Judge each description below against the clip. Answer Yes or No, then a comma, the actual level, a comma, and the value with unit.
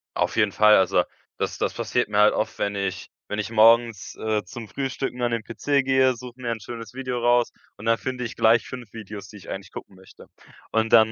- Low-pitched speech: Yes, low, 115 Hz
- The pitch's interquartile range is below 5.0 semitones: Yes, narrow, 2.5 semitones